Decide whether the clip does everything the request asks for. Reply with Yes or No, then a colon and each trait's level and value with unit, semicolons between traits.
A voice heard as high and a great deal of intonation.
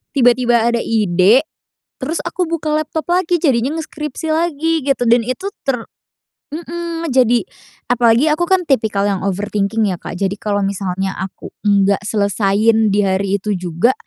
Yes: high, 230 Hz; wide, 7.3 semitones